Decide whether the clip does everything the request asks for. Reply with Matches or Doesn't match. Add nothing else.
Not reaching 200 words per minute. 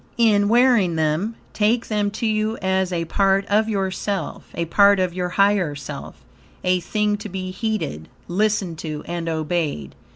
Matches